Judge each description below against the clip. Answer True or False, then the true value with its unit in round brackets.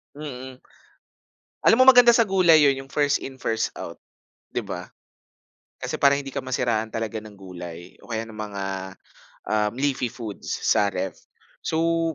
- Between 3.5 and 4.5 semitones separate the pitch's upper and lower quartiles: False (5.4 semitones)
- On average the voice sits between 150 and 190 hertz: False (125 Hz)